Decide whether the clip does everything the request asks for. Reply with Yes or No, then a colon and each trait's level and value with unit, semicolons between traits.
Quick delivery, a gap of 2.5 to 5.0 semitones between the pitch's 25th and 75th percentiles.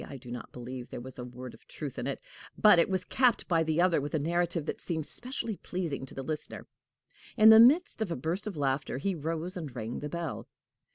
No: fast, 235 wpm; wide, 5.5 semitones